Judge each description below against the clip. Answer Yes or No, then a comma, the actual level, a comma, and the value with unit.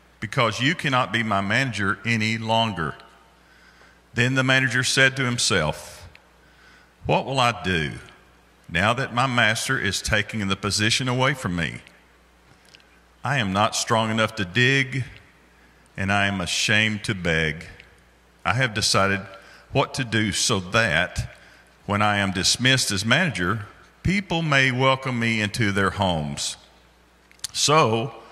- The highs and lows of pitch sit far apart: Yes, wide, 5.8 semitones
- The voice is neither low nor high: No, low, 105 Hz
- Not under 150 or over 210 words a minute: No, slow, 135 wpm